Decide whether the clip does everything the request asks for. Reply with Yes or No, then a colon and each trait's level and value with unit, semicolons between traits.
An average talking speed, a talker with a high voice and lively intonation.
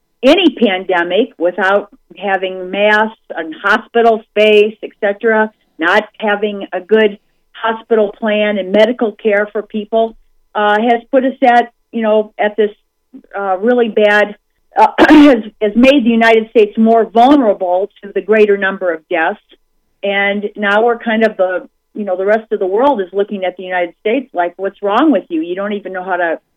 No: average, 175 wpm; high, 210 Hz; average, 2.7 semitones